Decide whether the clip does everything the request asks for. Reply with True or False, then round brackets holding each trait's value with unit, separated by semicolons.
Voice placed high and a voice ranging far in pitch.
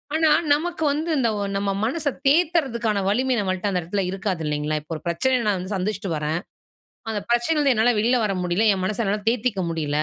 True (210 Hz; 5.8 semitones)